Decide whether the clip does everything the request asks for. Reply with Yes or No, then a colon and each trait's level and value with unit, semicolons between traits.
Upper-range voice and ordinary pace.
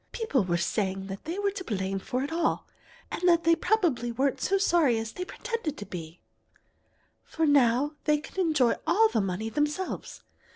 Yes: very high, 290 Hz; average, 180 wpm